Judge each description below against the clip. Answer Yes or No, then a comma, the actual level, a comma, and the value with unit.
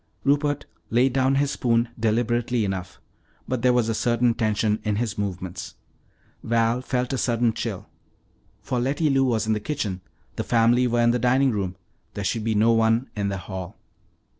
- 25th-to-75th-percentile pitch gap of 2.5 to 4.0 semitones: Yes, average, 2.8 semitones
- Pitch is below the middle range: Yes, low, 115 Hz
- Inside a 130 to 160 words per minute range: No, average, 180 wpm